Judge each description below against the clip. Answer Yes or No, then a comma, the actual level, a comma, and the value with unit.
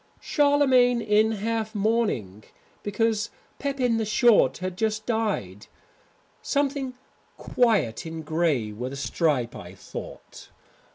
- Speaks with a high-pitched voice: Yes, high, 215 Hz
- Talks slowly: Yes, slow, 110 wpm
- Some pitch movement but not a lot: No, wide, 8.1 semitones